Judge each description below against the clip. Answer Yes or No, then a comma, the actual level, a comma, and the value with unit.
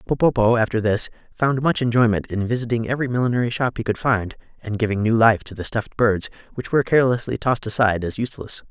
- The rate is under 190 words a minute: No, average, 200 wpm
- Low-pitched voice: Yes, low, 115 Hz